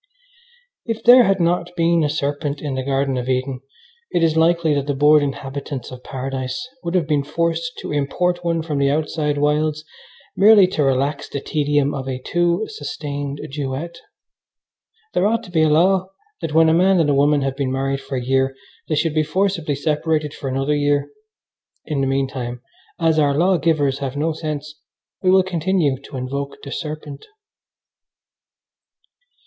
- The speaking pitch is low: No, medium, 150 Hz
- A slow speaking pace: No, average, 175 wpm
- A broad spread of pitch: No, average, 3.3 semitones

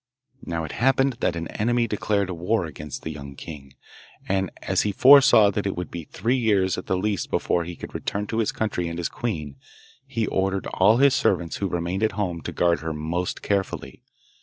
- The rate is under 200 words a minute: No, fast, 205 wpm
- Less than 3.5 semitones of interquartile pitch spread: No, average, 4.2 semitones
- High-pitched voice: No, very low, 95 Hz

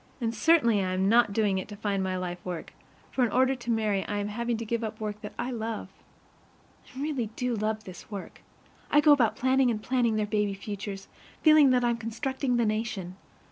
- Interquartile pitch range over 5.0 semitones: No, average, 3.1 semitones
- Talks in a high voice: Yes, high, 220 Hz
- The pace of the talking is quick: Yes, fast, 215 wpm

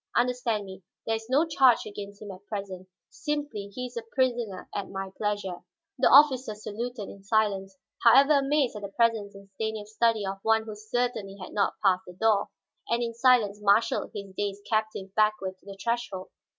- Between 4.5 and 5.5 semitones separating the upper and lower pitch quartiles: No, average, 3.2 semitones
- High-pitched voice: Yes, high, 215 Hz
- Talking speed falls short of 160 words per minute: No, average, 185 wpm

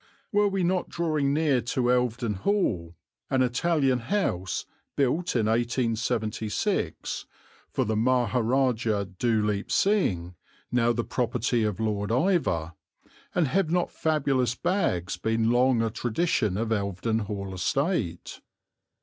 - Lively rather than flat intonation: No, average, 4.7 semitones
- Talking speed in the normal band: No, slow, 120 wpm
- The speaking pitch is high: No, low, 120 Hz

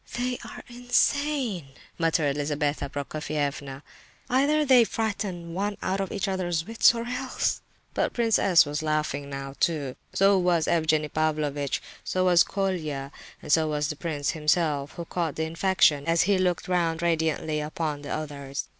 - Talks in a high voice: No, medium, 165 Hz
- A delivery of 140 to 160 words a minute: Yes, average, 155 wpm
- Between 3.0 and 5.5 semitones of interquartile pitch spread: Yes, average, 4.6 semitones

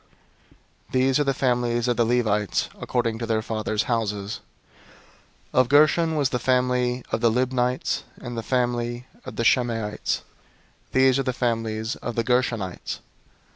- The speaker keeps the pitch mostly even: Yes, narrow, 2.1 semitones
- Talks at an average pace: Yes, average, 150 wpm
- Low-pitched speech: Yes, low, 120 Hz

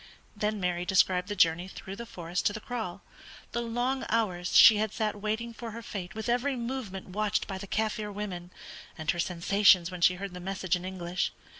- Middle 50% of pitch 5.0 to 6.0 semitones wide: No, average, 3.4 semitones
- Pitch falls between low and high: No, high, 200 Hz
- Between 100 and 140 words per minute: No, average, 200 wpm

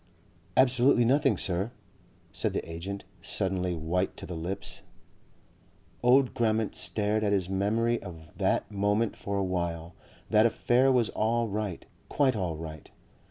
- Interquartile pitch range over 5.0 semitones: No, average, 4.4 semitones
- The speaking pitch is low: Yes, low, 100 Hz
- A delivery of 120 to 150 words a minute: Yes, average, 140 wpm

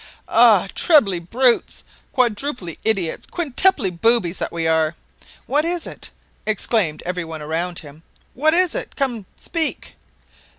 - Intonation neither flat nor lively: No, wide, 8.8 semitones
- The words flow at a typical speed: No, slow, 125 wpm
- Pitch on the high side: Yes, high, 215 Hz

